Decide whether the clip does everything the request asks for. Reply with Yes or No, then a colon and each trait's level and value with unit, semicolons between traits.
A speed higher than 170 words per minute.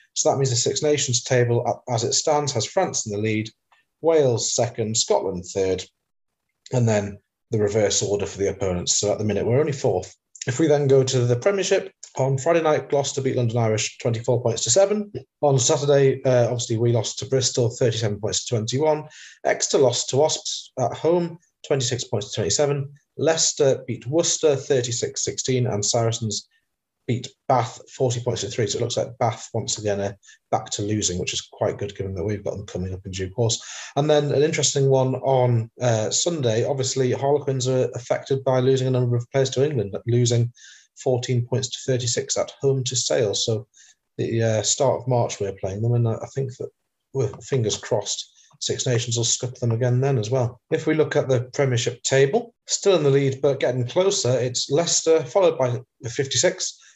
Yes: average, 195 wpm